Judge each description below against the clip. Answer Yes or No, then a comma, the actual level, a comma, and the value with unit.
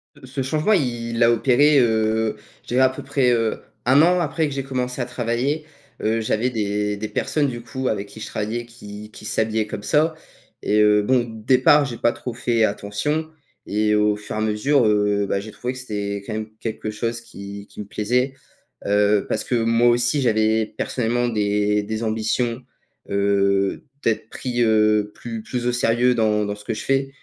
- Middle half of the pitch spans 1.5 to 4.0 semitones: Yes, average, 3.0 semitones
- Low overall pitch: Yes, low, 115 Hz